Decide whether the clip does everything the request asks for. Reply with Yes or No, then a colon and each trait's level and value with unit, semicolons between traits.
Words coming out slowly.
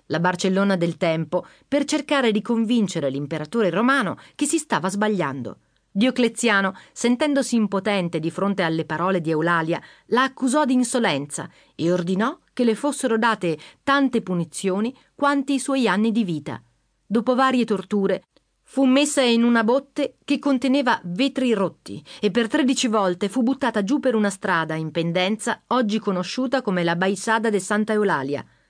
No: average, 155 wpm